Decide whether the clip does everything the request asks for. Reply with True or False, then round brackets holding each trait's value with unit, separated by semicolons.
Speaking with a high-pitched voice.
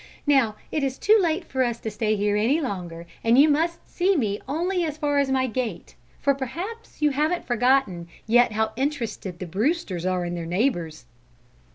True (255 Hz)